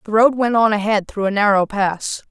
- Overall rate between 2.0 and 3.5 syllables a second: No, 5.2 syllables/s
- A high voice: Yes, high, 210 Hz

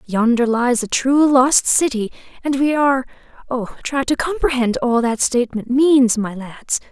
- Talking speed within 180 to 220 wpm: No, average, 155 wpm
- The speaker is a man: No, female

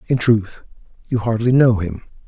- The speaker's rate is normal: Yes, average, 160 wpm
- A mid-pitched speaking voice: No, low, 110 Hz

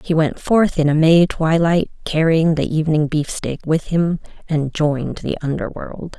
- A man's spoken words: No, female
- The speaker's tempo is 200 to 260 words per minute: No, average, 165 wpm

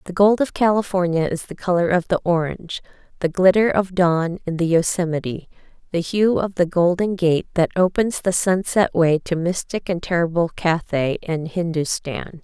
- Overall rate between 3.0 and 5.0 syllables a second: Yes, 4.8 syllables/s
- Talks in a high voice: No, medium, 175 Hz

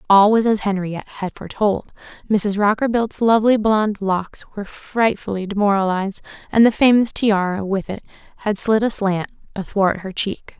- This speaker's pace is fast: No, average, 145 wpm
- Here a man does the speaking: No, female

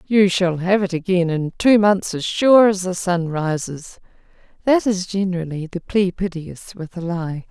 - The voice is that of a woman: Yes, female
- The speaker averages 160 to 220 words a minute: Yes, average, 185 wpm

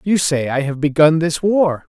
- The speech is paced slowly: No, fast, 215 wpm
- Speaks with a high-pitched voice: No, medium, 160 Hz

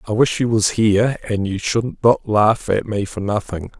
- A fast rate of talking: Yes, fast, 220 wpm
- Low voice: Yes, low, 105 Hz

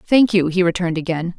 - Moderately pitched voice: Yes, medium, 180 Hz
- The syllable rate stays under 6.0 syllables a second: No, 6.2 syllables/s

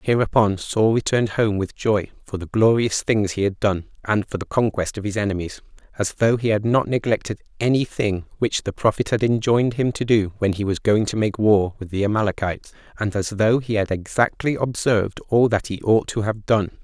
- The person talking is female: No, male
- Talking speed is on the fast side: Yes, fast, 215 wpm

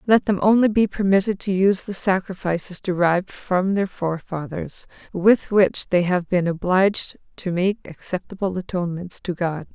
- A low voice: No, medium, 185 Hz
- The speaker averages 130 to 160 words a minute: Yes, average, 155 wpm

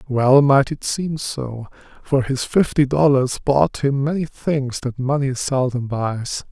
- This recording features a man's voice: Yes, male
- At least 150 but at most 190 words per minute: Yes, average, 155 wpm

